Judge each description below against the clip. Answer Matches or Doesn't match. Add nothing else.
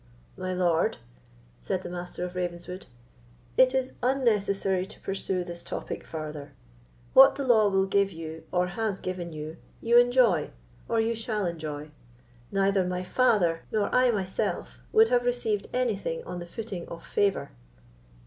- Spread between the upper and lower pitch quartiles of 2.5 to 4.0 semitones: Doesn't match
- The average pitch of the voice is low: Doesn't match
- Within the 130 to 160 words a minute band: Matches